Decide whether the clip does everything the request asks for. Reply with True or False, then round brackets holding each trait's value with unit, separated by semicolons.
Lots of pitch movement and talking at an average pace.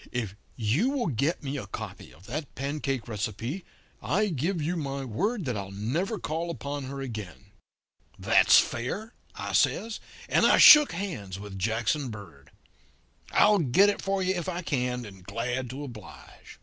True (8.0 semitones; 165 wpm)